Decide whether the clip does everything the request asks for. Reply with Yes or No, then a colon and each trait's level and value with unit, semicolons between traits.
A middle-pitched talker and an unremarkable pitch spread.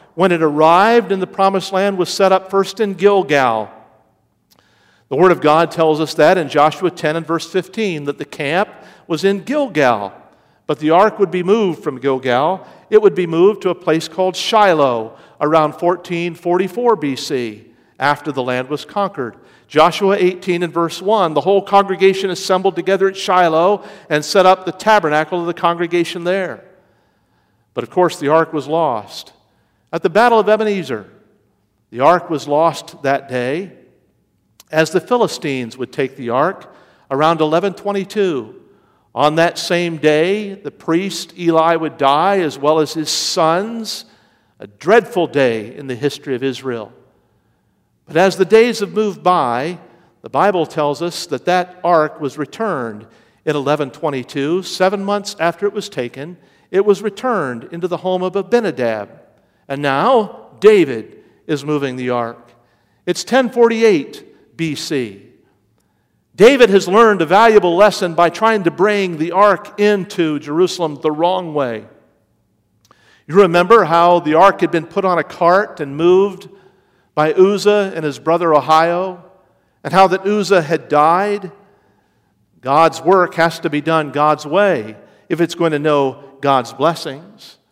Yes: medium, 175 Hz; average, 4.4 semitones